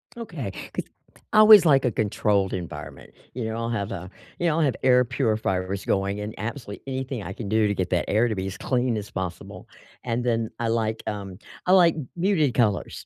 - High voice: No, low, 115 Hz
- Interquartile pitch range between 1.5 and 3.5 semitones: No, average, 4.6 semitones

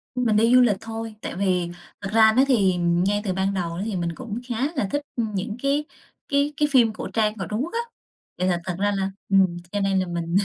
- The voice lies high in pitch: Yes, high, 205 Hz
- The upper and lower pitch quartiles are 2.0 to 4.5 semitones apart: Yes, average, 4.0 semitones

